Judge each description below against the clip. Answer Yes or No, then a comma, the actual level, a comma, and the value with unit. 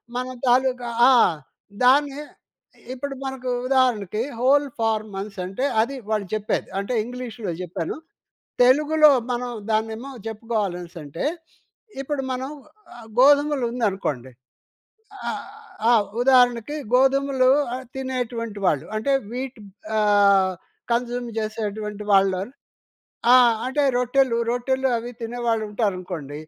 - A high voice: Yes, high, 240 Hz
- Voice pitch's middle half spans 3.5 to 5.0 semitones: Yes, average, 3.8 semitones